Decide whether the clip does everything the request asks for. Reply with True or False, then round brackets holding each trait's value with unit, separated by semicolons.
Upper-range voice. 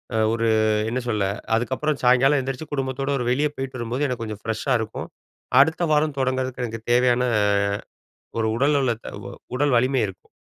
False (130 Hz)